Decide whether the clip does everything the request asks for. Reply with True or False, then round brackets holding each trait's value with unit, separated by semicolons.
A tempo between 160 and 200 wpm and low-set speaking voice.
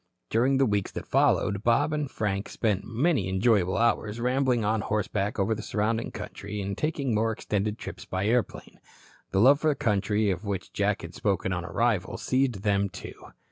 True (180 wpm; 105 Hz)